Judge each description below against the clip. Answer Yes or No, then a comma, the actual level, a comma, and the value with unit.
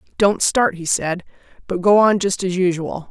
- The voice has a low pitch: No, medium, 185 Hz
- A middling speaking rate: Yes, average, 195 wpm